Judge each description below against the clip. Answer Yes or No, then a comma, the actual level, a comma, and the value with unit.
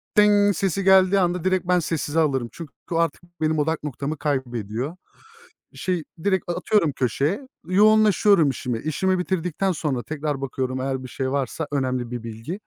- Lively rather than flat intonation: Yes, wide, 5.9 semitones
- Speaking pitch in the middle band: Yes, medium, 155 Hz